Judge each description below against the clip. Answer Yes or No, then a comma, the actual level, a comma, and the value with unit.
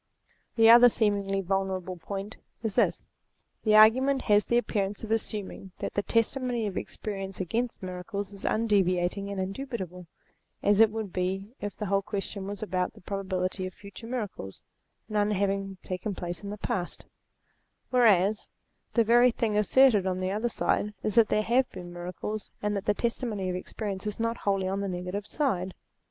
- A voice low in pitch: No, high, 200 Hz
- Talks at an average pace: Yes, average, 170 wpm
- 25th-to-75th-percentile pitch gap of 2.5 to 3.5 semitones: Yes, average, 2.8 semitones